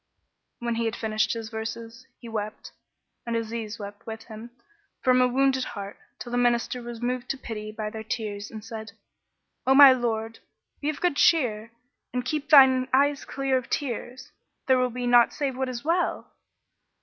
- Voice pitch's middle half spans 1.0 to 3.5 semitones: Yes, average, 2.8 semitones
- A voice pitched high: Yes, high, 240 Hz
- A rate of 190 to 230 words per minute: No, average, 180 wpm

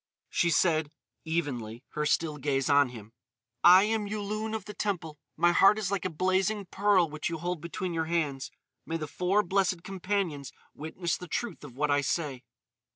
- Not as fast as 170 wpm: No, average, 180 wpm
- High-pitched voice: No, medium, 170 Hz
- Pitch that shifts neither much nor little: Yes, average, 4.5 semitones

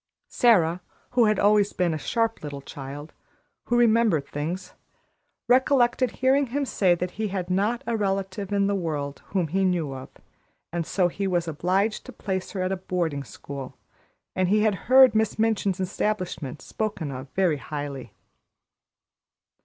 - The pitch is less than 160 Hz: No, medium, 185 Hz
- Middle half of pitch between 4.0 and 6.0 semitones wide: Yes, average, 5.1 semitones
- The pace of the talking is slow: No, average, 160 wpm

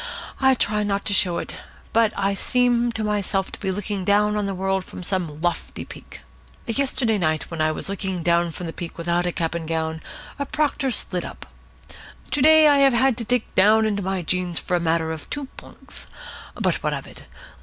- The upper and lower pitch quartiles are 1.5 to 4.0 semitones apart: No, average, 4.7 semitones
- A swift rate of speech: Yes, fast, 210 wpm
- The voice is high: Yes, high, 195 Hz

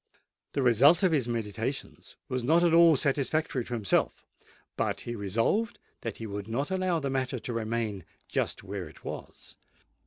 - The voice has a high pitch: No, low, 130 Hz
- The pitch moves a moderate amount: No, wide, 5.7 semitones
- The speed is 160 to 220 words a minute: Yes, average, 165 wpm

